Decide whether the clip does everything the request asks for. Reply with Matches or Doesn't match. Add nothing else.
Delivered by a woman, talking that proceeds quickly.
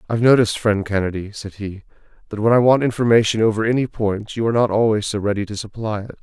Doesn't match